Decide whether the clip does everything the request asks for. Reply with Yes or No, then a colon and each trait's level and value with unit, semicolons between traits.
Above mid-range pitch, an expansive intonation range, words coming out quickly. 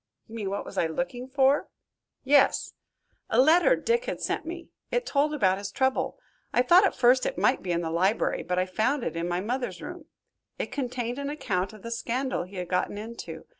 Yes: high, 245 Hz; wide, 6.7 semitones; fast, 210 wpm